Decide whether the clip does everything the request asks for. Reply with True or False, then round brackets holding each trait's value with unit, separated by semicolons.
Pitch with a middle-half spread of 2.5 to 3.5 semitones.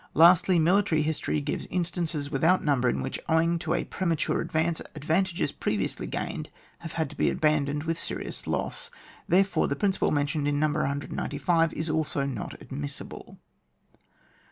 True (2.8 semitones)